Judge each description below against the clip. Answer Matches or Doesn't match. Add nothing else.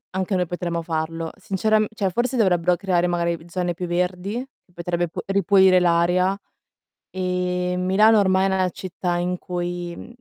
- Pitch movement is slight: Matches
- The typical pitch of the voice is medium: Matches